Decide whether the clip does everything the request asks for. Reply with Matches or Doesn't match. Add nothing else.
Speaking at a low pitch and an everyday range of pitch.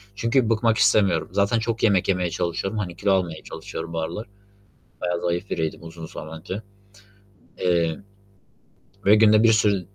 Matches